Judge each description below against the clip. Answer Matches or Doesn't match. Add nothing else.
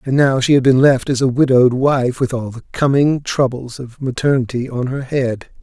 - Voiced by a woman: Doesn't match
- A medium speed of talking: Doesn't match